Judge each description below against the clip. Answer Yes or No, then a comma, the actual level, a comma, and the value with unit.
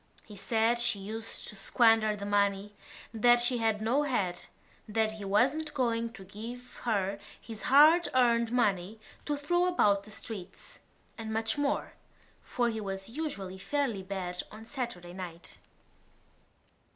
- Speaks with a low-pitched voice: No, high, 220 Hz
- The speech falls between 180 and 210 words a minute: No, average, 150 wpm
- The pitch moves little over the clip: No, average, 3.5 semitones